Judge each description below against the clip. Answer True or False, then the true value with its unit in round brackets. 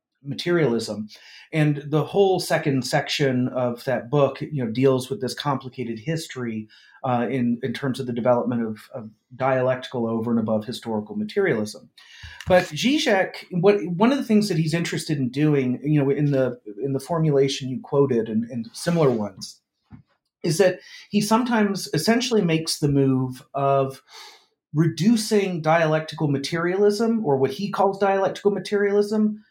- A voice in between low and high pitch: True (145 Hz)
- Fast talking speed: False (150 wpm)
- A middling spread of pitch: False (6.9 semitones)